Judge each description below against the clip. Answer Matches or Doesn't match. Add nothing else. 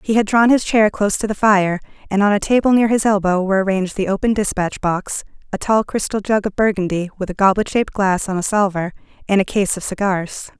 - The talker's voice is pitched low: Doesn't match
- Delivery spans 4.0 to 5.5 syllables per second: Doesn't match